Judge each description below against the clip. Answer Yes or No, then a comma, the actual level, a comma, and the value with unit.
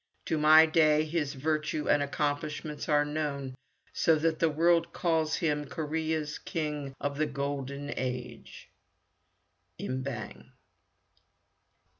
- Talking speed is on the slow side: Yes, slow, 115 wpm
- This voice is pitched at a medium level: Yes, medium, 150 Hz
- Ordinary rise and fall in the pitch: No, narrow, 1.9 semitones